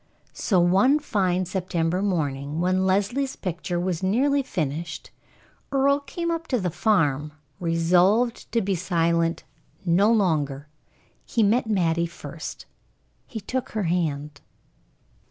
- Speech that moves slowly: Yes, slow, 120 wpm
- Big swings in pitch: No, average, 4.9 semitones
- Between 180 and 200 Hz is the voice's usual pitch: Yes, medium, 185 Hz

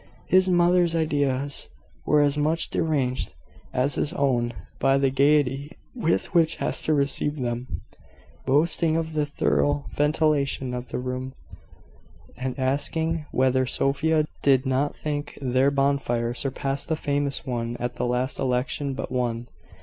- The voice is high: No, medium, 140 Hz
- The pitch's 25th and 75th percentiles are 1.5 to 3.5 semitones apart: Yes, average, 2.8 semitones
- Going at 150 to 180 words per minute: No, slow, 135 wpm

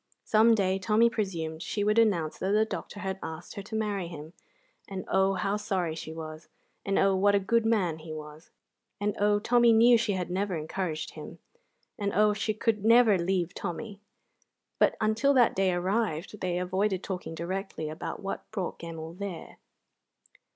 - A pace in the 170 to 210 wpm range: Yes, average, 175 wpm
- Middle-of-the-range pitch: No, high, 195 Hz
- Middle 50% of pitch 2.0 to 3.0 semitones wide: No, average, 3.5 semitones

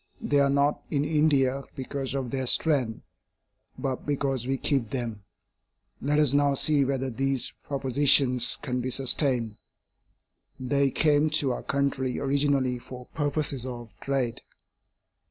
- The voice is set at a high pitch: No, low, 135 Hz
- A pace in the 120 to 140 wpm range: Yes, slow, 135 wpm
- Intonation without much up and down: Yes, narrow, 2.0 semitones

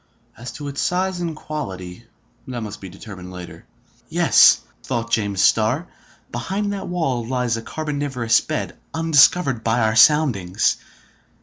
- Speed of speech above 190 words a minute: No, slow, 135 wpm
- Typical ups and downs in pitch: No, wide, 6.1 semitones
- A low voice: Yes, low, 125 Hz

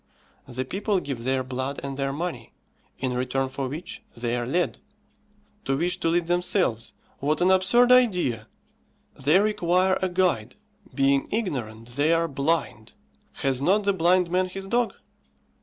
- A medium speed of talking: Yes, average, 155 wpm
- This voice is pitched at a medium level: Yes, medium, 155 Hz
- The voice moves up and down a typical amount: No, wide, 5.9 semitones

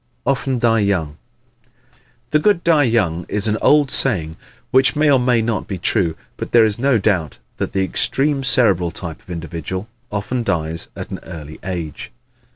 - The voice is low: Yes, low, 105 Hz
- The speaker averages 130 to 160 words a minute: No, average, 175 wpm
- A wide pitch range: Yes, wide, 6.9 semitones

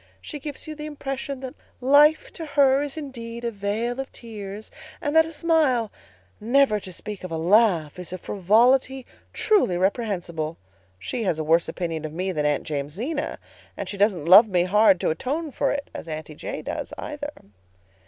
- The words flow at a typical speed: Yes, average, 185 wpm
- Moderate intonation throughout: No, wide, 7.5 semitones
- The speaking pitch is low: No, high, 225 Hz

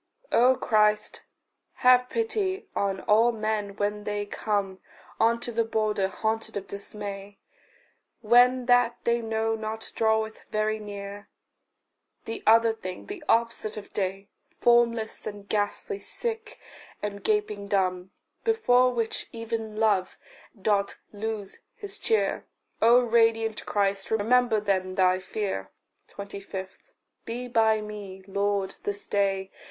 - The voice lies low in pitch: No, high, 215 Hz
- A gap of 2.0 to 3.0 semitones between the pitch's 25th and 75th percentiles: Yes, narrow, 2.6 semitones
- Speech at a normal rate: No, slow, 120 wpm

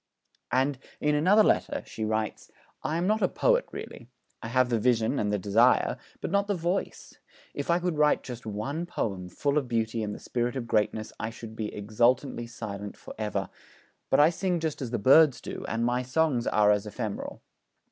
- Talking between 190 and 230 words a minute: Yes, average, 200 wpm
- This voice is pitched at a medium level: No, low, 120 Hz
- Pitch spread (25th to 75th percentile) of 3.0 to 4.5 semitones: No, wide, 5.6 semitones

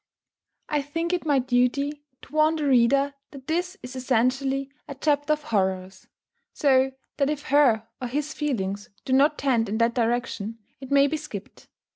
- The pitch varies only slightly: No, average, 3.7 semitones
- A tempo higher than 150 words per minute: Yes, average, 170 wpm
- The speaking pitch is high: Yes, very high, 275 Hz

